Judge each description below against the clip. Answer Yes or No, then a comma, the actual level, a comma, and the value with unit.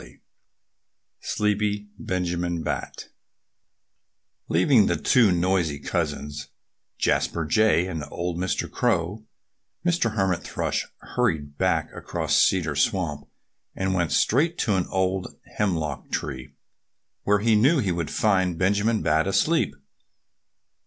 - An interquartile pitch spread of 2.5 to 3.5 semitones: No, average, 3.9 semitones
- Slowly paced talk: Yes, slow, 115 wpm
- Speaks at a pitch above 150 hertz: No, very low, 95 Hz